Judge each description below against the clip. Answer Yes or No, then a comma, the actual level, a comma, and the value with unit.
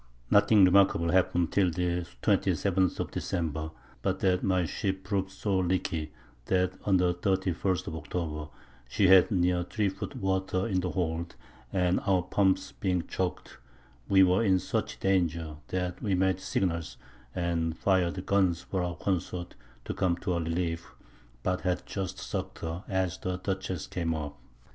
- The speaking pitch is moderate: No, very low, 90 Hz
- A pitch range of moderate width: No, narrow, 1.8 semitones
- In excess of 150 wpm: Yes, average, 160 wpm